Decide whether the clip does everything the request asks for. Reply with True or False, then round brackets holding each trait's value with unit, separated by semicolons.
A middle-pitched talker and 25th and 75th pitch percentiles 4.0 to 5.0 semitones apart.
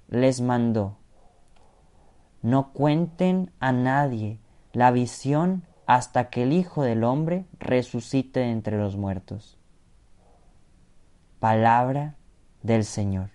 False (120 Hz; 4.7 semitones)